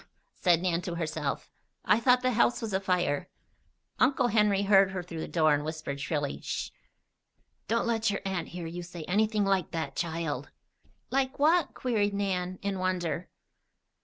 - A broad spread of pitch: No, average, 4.2 semitones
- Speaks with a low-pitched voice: No, medium, 185 Hz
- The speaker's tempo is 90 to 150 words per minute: No, average, 160 wpm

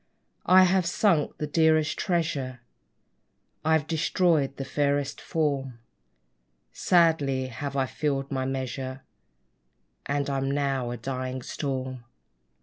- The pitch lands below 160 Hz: Yes, medium, 140 Hz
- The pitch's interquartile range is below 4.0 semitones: Yes, average, 3.1 semitones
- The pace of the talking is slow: Yes, slow, 110 wpm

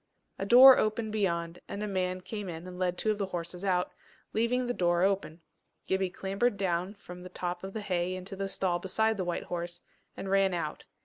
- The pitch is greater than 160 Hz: Yes, high, 190 Hz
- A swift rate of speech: Yes, fast, 210 wpm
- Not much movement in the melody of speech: Yes, narrow, 2.3 semitones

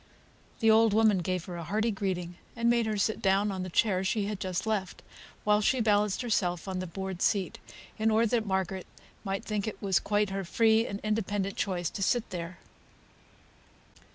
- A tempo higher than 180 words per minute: Yes, average, 190 wpm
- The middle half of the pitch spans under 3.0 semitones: Yes, narrow, 2.6 semitones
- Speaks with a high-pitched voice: Yes, high, 200 Hz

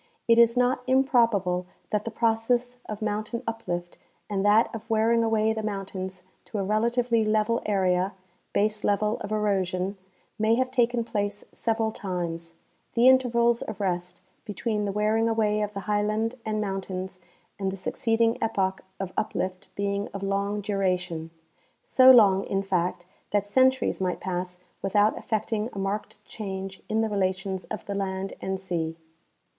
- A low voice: No, high, 210 Hz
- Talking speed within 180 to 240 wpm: No, average, 160 wpm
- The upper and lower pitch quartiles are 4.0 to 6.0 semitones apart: No, average, 2.9 semitones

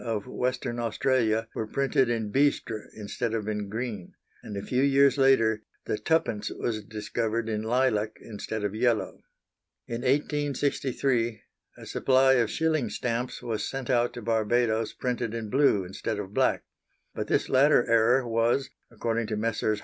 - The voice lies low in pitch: Yes, low, 115 Hz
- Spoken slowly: No, average, 155 wpm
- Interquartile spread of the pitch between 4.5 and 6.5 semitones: No, average, 3.0 semitones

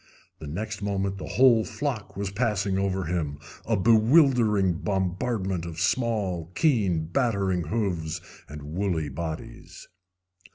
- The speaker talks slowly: Yes, slow, 120 wpm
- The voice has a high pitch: No, very low, 95 Hz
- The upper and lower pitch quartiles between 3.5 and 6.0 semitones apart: Yes, average, 4.4 semitones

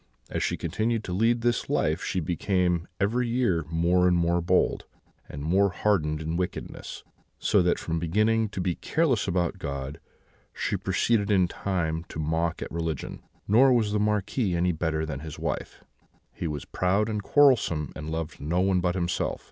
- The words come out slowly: No, average, 175 wpm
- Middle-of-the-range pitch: No, very low, 90 Hz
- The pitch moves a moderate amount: Yes, average, 4.3 semitones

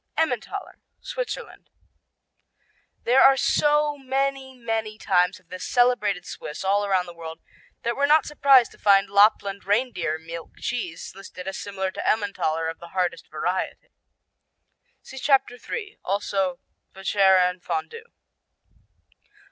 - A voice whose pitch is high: Yes, high, 200 Hz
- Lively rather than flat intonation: Yes, wide, 6.3 semitones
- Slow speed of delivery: Yes, slow, 125 wpm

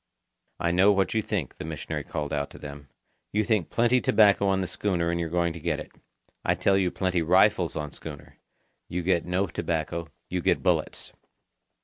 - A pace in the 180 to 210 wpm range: Yes, average, 195 wpm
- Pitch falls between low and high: No, very low, 90 Hz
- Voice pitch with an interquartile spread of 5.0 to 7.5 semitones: No, average, 3.4 semitones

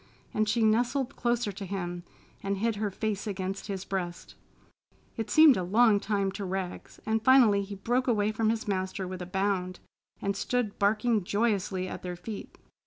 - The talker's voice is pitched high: Yes, high, 205 Hz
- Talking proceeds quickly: No, average, 175 wpm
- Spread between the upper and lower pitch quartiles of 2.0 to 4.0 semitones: Yes, average, 2.7 semitones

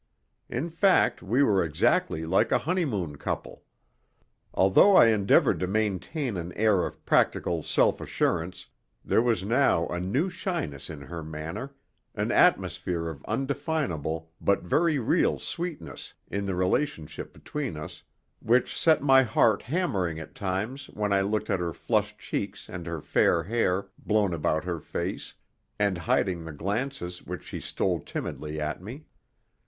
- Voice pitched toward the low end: Yes, very low, 95 Hz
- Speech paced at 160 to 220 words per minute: No, average, 150 wpm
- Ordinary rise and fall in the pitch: No, wide, 7.4 semitones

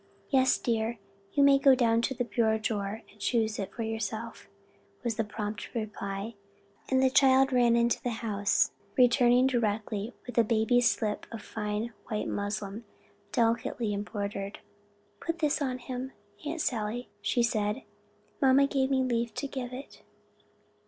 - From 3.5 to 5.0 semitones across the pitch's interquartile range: No, average, 3.1 semitones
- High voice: Yes, high, 235 Hz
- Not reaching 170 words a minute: Yes, average, 145 wpm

